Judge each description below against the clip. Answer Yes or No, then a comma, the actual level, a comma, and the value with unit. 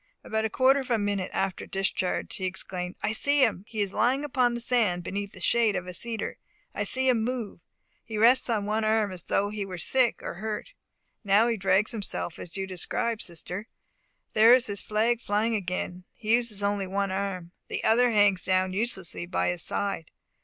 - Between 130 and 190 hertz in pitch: No, high, 205 Hz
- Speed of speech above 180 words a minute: Yes, fast, 205 wpm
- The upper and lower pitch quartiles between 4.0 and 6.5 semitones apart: No, average, 3.6 semitones